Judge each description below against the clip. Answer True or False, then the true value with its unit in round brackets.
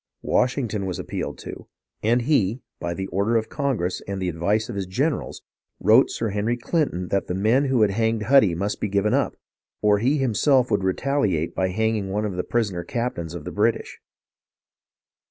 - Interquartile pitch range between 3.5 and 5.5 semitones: True (4.2 semitones)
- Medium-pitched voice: False (105 Hz)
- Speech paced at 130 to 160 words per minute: False (185 wpm)